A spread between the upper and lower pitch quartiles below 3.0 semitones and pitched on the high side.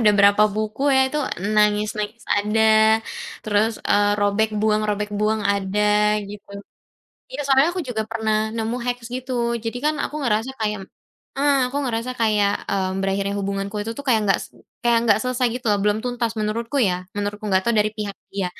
Yes: narrow, 2.4 semitones; high, 215 Hz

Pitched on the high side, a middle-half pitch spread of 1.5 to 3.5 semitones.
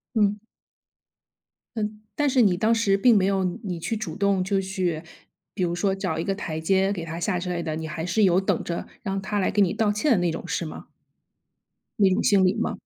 Yes: high, 195 Hz; average, 2.9 semitones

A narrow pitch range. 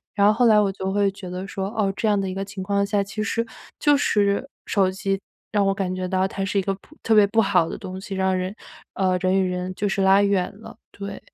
Yes: narrow, 1.3 semitones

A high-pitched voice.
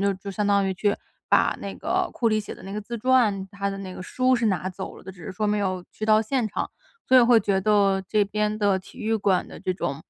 Yes: high, 205 Hz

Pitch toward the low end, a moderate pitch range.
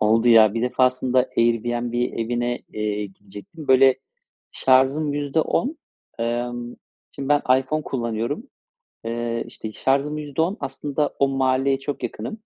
Yes: low, 130 Hz; average, 3.1 semitones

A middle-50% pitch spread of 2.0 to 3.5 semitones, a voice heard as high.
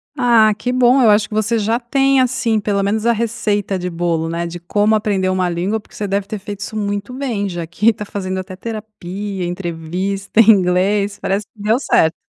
Yes: average, 2.9 semitones; high, 205 Hz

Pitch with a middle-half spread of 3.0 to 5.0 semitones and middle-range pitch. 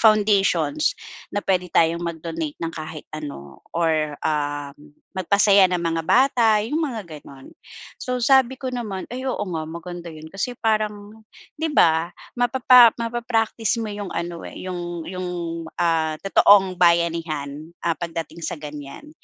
No: wide, 5.4 semitones; medium, 180 Hz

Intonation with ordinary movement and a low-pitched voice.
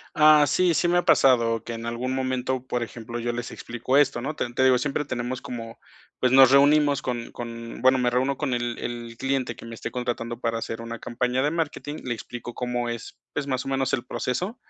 No: narrow, 2.2 semitones; low, 125 Hz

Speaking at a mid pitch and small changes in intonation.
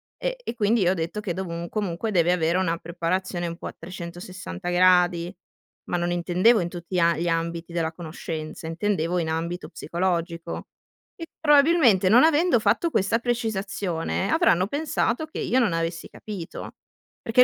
No: medium, 180 Hz; average, 4.3 semitones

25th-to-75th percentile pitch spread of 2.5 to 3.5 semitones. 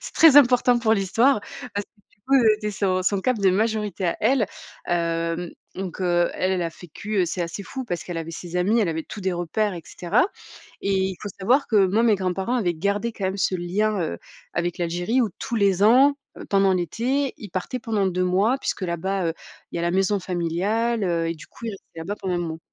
No: average, 4.0 semitones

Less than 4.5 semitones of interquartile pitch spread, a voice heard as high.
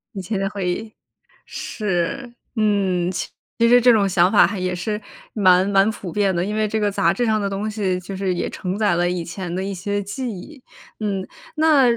Yes: average, 2.8 semitones; high, 200 Hz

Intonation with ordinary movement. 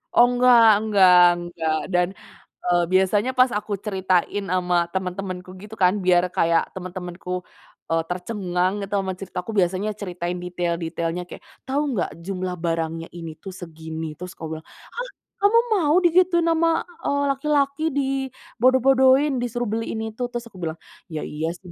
No: wide, 5.8 semitones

